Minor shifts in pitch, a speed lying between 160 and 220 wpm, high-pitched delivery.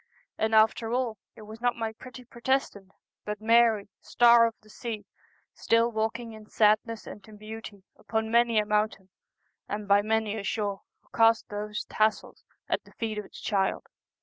Yes: narrow, 1.5 semitones; average, 175 wpm; high, 220 Hz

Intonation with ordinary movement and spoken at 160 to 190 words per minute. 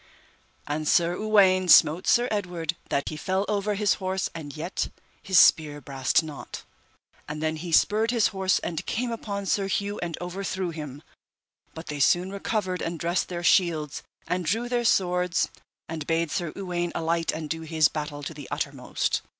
Yes: average, 3.7 semitones; average, 175 wpm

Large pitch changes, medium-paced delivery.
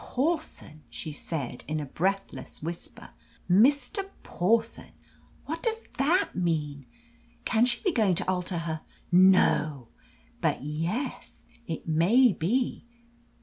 No: wide, 7.8 semitones; slow, 115 wpm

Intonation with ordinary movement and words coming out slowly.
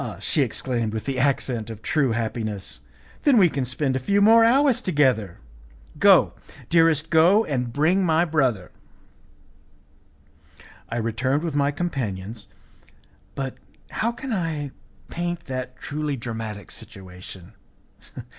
No: wide, 6.4 semitones; slow, 125 wpm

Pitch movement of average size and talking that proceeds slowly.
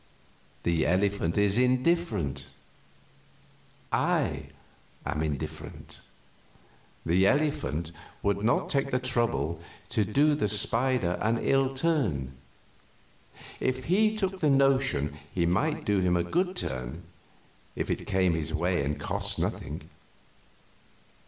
No: wide, 8.2 semitones; slow, 120 wpm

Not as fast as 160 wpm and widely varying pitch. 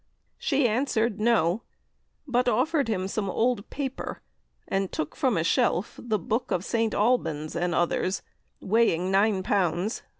No: average, 140 wpm; average, 4.5 semitones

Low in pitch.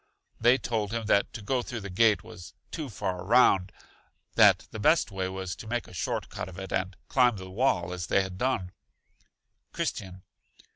Yes: low, 100 Hz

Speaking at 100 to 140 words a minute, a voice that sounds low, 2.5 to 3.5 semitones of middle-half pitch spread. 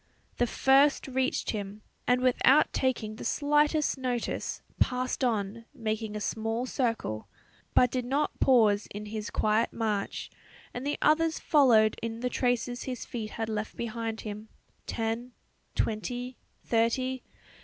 No: slow, 135 wpm; high, 235 Hz; average, 2.9 semitones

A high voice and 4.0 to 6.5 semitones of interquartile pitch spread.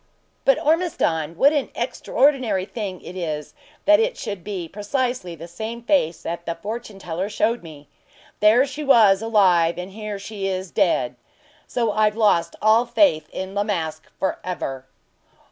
Yes: high, 205 Hz; wide, 5.4 semitones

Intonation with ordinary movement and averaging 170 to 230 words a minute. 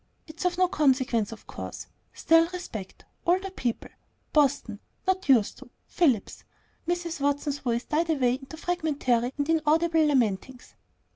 No: average, 5.0 semitones; average, 140 wpm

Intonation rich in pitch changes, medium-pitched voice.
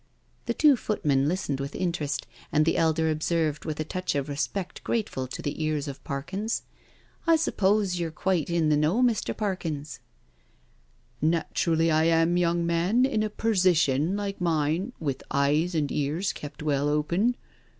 No: average, 4.2 semitones; medium, 165 Hz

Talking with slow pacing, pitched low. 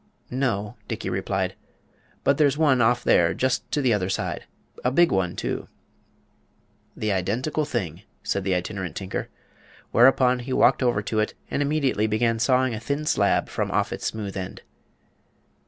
No: average, 160 wpm; low, 120 Hz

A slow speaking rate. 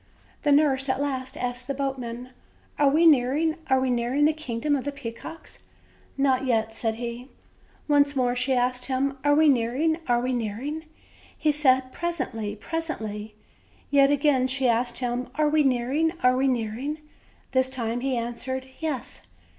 No: average, 160 wpm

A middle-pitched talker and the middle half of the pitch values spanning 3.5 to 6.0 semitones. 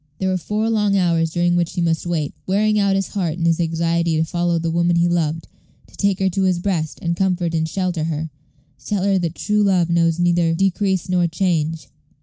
No: medium, 175 Hz; narrow, 2.5 semitones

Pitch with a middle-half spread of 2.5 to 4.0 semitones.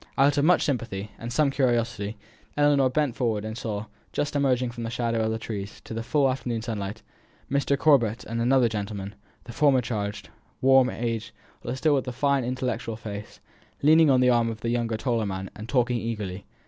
Yes: average, 3.2 semitones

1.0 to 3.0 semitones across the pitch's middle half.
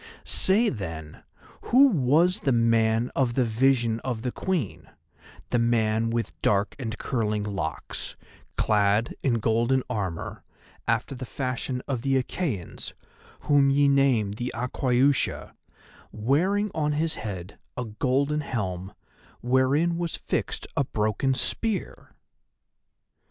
No: average, 4.2 semitones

